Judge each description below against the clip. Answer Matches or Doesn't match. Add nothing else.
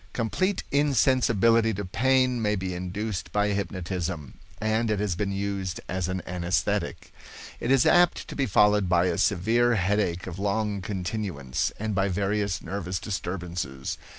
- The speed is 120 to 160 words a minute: Matches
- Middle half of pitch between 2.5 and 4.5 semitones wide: Matches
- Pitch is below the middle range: Matches